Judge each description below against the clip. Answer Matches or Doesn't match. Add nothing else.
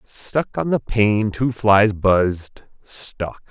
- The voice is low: Matches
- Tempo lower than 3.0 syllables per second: Matches